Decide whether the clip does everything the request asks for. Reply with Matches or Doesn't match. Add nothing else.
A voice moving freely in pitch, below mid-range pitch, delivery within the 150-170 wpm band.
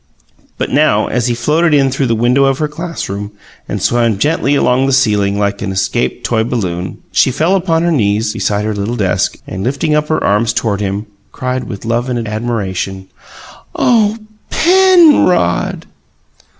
Matches